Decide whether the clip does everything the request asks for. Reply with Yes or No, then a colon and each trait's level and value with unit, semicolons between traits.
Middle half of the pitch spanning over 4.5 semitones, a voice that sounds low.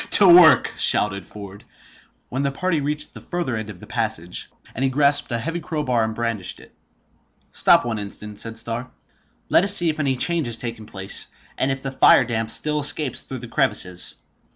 Yes: average, 5.2 semitones; low, 125 Hz